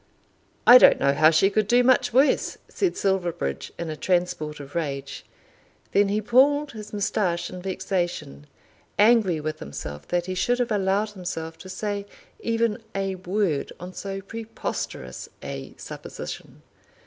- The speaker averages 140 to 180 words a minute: Yes, average, 150 wpm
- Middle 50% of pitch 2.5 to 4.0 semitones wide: No, average, 4.8 semitones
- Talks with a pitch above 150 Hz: Yes, high, 190 Hz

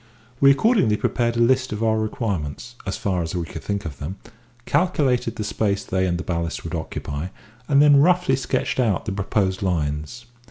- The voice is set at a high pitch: No, low, 105 Hz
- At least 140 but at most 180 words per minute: No, average, 190 wpm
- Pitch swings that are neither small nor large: No, wide, 6.2 semitones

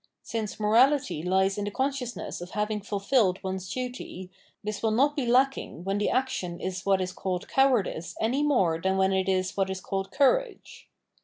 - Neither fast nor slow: Yes, average, 180 wpm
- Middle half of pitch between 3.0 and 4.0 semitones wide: No, average, 5.1 semitones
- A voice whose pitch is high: Yes, high, 205 Hz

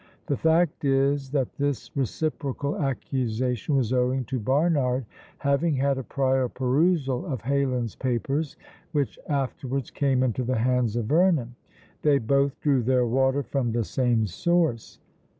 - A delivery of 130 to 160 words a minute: Yes, average, 140 wpm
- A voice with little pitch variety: Yes, narrow, 2.2 semitones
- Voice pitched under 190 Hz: Yes, low, 135 Hz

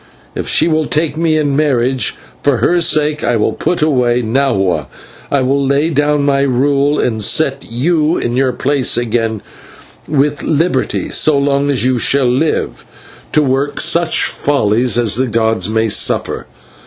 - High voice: No, medium, 140 Hz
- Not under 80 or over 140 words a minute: No, average, 160 wpm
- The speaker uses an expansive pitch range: No, average, 3.6 semitones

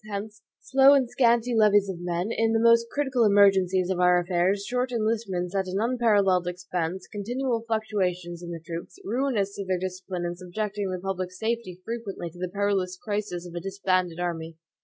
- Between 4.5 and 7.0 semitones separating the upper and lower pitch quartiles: No, average, 3.8 semitones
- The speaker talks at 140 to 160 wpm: No, average, 180 wpm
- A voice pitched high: Yes, high, 195 Hz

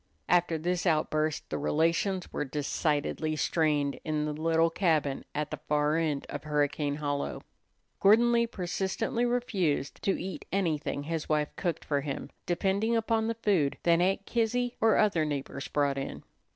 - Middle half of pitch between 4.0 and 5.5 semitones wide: Yes, average, 4.7 semitones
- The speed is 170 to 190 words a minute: No, average, 155 wpm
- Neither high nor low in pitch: Yes, medium, 160 Hz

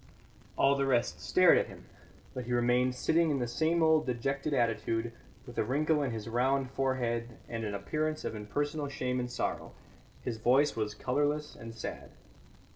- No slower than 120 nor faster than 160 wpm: No, average, 175 wpm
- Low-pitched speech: Yes, low, 125 Hz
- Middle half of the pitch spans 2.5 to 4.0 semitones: Yes, average, 3.7 semitones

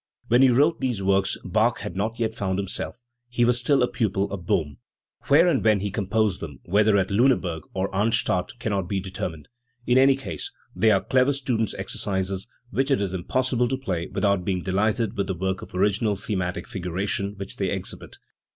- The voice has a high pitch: No, low, 100 Hz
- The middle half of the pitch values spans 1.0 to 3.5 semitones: No, average, 4.1 semitones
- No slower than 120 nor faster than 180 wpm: No, average, 195 wpm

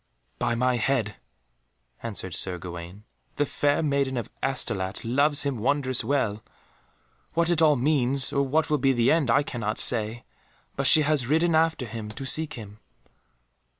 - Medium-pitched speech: No, low, 130 Hz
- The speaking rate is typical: Yes, average, 160 wpm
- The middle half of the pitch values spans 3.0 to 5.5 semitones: Yes, average, 4.5 semitones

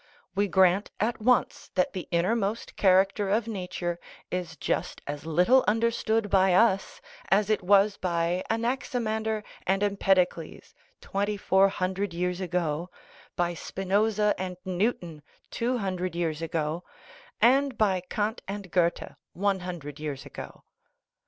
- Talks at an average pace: No, slow, 130 wpm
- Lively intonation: No, average, 3.2 semitones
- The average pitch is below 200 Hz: Yes, high, 190 Hz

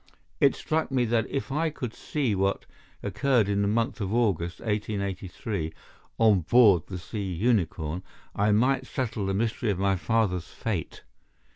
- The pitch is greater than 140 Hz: No, low, 105 Hz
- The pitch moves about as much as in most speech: Yes, average, 3.7 semitones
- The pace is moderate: Yes, average, 155 wpm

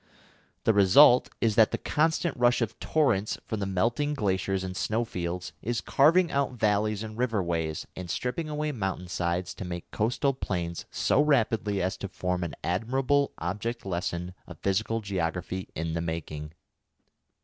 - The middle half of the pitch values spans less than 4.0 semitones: No, average, 5.3 semitones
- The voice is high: No, low, 100 Hz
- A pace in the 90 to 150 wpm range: No, average, 160 wpm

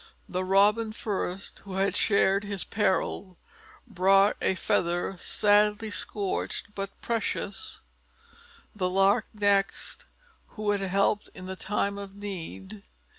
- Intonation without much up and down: Yes, narrow, 1.4 semitones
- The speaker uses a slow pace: Yes, slow, 120 wpm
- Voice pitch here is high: Yes, high, 200 Hz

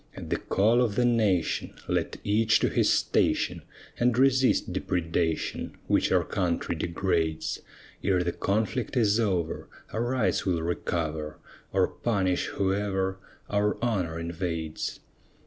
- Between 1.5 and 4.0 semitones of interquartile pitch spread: No, average, 4.6 semitones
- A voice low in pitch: Yes, very low, 95 Hz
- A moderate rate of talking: No, slow, 130 wpm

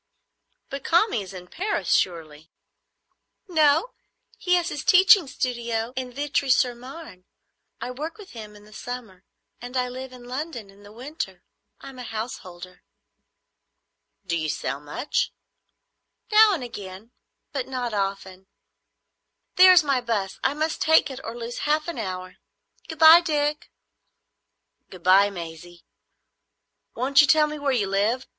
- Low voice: No, very high, 250 Hz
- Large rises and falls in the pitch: Yes, wide, 7.2 semitones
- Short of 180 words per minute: Yes, average, 150 wpm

